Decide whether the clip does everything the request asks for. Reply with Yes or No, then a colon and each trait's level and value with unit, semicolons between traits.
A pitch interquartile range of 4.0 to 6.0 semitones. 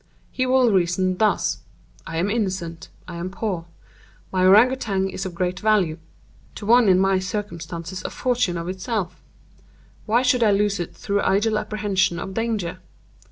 No: average, 3.3 semitones